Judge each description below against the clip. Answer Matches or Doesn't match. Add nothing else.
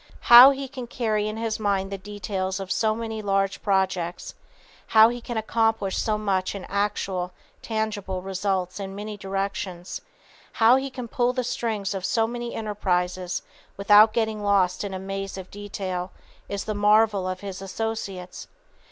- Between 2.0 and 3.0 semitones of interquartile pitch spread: Matches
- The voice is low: Doesn't match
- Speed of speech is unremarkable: Matches